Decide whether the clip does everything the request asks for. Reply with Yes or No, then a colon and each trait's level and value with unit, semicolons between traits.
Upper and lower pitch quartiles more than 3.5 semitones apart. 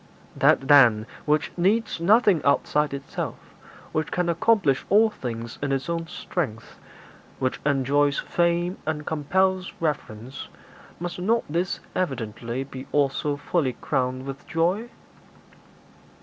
Yes: average, 4.6 semitones